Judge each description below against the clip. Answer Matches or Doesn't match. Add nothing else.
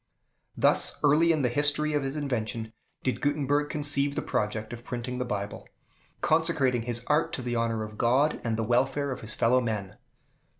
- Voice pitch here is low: Matches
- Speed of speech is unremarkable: Matches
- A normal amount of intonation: Matches